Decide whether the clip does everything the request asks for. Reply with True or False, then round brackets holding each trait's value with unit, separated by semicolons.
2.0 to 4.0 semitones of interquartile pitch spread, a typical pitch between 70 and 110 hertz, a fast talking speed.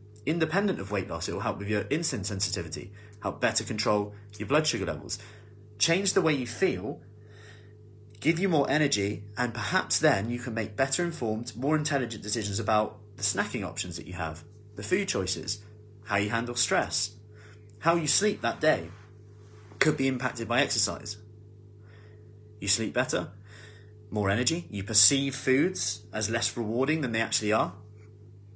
False (3.0 semitones; 105 Hz; 160 wpm)